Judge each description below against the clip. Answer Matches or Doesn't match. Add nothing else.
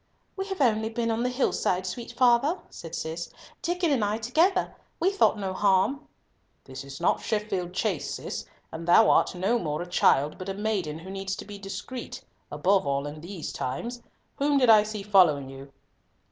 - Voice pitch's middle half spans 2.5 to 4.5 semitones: Doesn't match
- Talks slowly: Doesn't match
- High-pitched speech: Matches